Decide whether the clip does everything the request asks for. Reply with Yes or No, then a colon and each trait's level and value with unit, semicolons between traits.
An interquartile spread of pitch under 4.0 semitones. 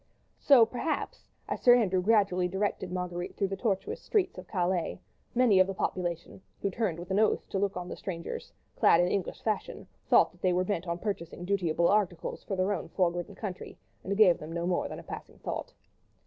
Yes: average, 2.7 semitones